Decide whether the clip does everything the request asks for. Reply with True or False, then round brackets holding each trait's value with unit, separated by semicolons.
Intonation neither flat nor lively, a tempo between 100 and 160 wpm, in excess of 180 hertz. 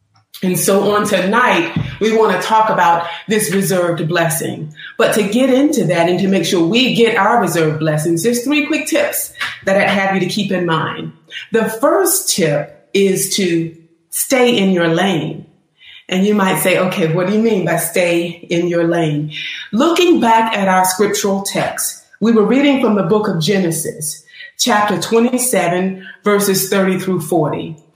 False (4.4 semitones; 175 wpm; 190 Hz)